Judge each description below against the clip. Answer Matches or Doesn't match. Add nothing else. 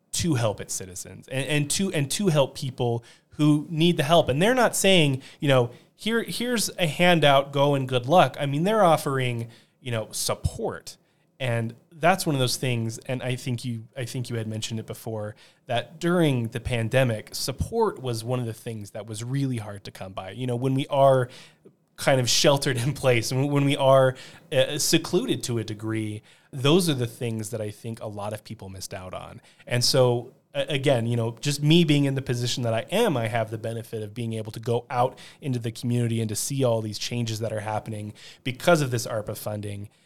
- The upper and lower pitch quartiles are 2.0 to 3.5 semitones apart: Doesn't match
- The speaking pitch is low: Matches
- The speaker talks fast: Matches